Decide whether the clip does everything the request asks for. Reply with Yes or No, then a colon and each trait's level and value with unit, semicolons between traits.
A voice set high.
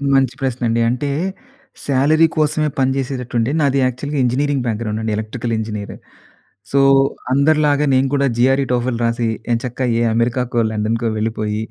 No: low, 125 Hz